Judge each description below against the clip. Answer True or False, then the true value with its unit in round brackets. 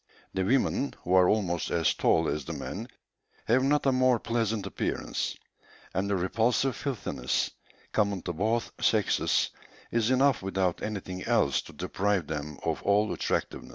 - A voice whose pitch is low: True (105 Hz)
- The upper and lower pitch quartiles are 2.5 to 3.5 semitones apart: False (4.4 semitones)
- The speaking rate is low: False (155 wpm)